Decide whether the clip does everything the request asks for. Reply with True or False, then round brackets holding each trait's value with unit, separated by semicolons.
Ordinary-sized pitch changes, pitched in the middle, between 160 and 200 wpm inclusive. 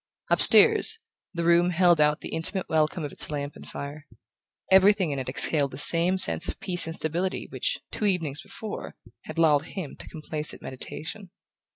True (3.5 semitones; 165 Hz; 175 wpm)